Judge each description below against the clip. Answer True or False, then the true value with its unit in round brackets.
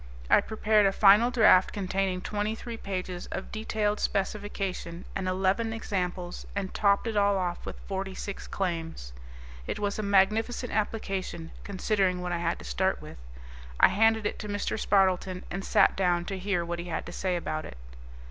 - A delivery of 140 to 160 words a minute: False (175 wpm)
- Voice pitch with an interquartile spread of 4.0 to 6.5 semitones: False (2.5 semitones)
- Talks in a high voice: True (195 Hz)